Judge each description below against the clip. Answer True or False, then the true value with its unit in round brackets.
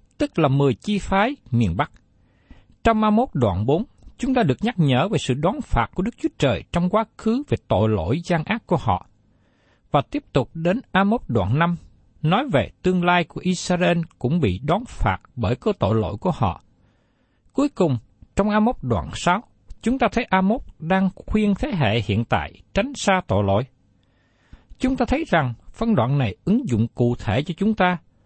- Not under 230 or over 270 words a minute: False (200 wpm)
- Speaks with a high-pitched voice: False (170 Hz)